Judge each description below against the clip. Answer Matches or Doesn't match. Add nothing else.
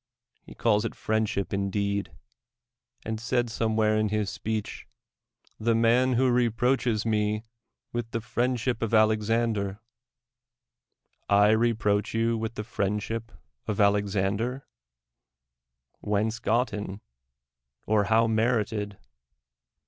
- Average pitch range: Doesn't match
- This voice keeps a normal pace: Doesn't match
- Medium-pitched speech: Doesn't match